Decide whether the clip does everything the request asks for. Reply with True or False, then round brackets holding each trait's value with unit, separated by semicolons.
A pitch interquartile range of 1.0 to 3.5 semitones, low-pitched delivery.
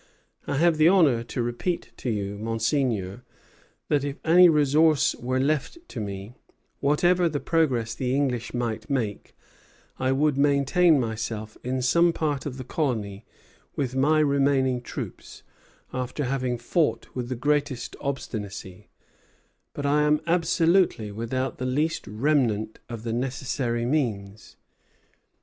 False (4.3 semitones; 130 Hz)